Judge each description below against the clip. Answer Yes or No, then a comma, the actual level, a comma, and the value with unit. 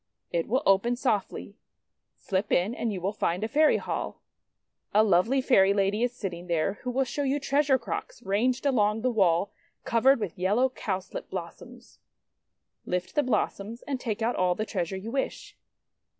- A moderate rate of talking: Yes, average, 170 wpm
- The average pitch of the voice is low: No, high, 215 Hz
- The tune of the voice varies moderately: Yes, average, 4.8 semitones